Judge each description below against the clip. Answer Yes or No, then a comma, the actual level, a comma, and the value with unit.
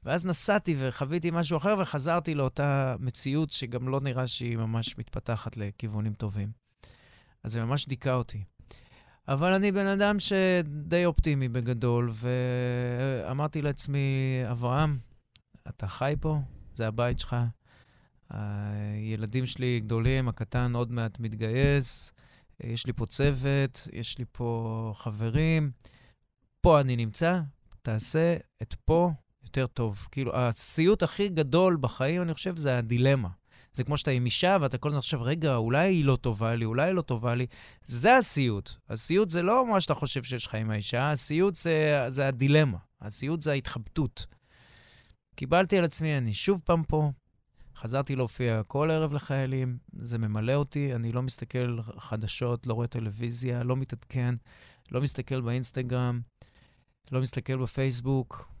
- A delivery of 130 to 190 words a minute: Yes, average, 140 wpm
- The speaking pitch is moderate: No, low, 130 Hz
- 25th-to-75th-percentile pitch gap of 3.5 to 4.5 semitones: Yes, average, 4.1 semitones